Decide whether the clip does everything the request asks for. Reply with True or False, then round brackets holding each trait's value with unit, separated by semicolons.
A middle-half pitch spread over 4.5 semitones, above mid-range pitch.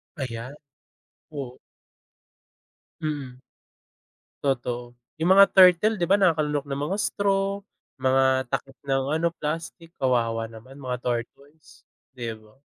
False (4.9 semitones; 135 Hz)